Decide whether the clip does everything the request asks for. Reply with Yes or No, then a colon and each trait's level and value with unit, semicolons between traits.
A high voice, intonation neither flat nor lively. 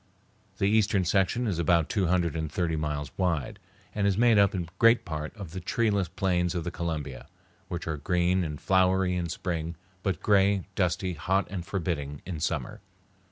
No: very low, 90 Hz; average, 3.0 semitones